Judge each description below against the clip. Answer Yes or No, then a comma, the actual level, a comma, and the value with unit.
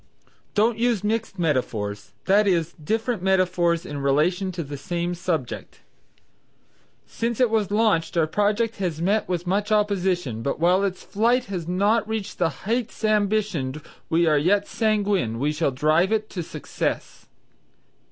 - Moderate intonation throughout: Yes, average, 4.6 semitones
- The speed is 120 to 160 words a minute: Yes, average, 150 wpm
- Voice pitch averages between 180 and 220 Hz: Yes, medium, 185 Hz